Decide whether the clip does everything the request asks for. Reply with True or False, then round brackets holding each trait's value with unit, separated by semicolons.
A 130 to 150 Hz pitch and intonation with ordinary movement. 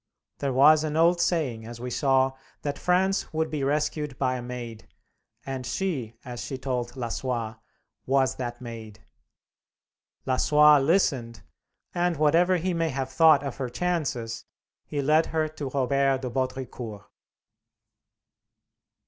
True (135 Hz; 3.9 semitones)